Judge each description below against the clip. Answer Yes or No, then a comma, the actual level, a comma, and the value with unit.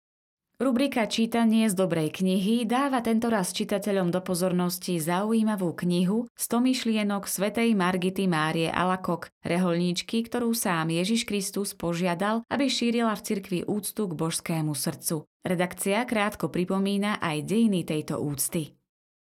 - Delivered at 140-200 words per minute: No, average, 120 wpm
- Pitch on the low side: No, high, 195 Hz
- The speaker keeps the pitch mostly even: No, average, 4.2 semitones